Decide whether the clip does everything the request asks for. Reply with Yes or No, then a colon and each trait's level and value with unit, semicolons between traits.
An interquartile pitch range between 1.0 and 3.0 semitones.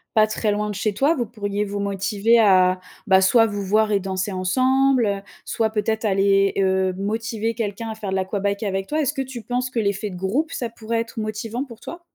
Yes: average, 2.7 semitones